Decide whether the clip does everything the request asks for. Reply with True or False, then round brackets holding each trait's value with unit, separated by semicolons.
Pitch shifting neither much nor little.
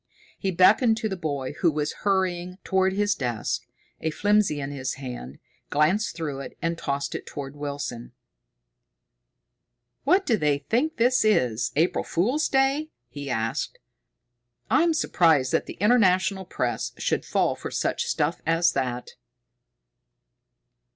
False (6.7 semitones)